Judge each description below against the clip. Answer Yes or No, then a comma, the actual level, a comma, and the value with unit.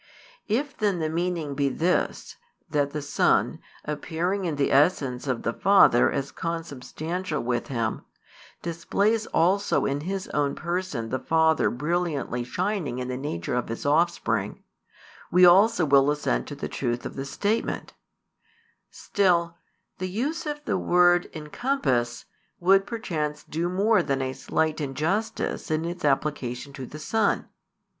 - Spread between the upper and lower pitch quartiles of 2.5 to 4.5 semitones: No, average, 5.0 semitones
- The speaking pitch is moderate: Yes, medium, 160 Hz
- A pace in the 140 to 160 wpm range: Yes, average, 145 wpm